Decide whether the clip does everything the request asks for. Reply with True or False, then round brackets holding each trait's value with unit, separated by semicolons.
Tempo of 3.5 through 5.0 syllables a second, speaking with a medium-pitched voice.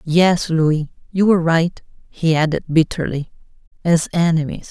True (4.5 syllables/s; 165 Hz)